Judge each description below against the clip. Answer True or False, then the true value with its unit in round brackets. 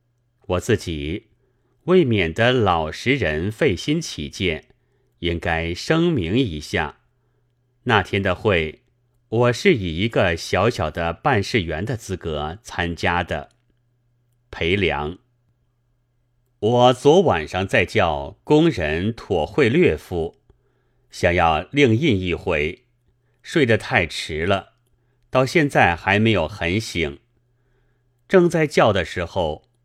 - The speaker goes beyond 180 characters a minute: False (160 characters per minute)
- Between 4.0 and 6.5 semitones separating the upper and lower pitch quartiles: True (5.7 semitones)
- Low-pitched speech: True (120 Hz)